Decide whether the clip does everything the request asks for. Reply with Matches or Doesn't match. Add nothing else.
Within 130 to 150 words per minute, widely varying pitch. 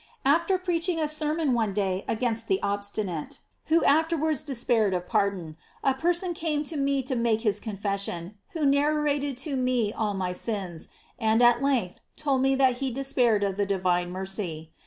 Doesn't match